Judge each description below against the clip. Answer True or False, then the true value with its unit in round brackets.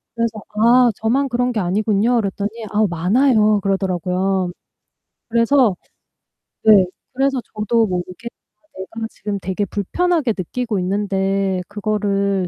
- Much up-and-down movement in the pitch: False (3.2 semitones)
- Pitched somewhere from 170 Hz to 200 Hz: False (210 Hz)